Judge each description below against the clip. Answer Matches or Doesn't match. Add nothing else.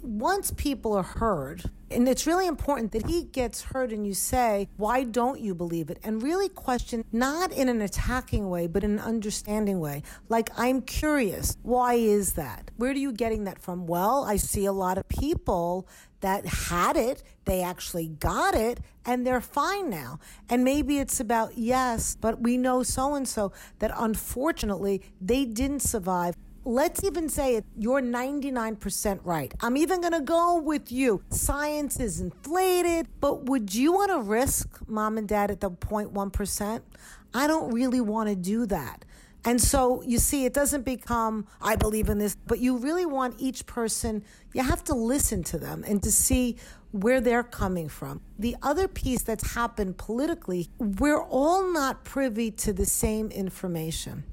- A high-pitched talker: Matches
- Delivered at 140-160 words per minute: Doesn't match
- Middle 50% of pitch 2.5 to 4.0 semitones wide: Doesn't match